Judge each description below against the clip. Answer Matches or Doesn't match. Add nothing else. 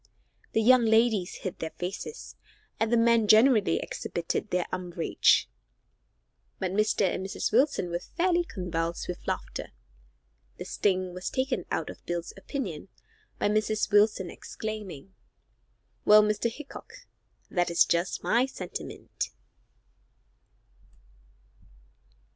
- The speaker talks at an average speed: Doesn't match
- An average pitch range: Matches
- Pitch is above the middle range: Matches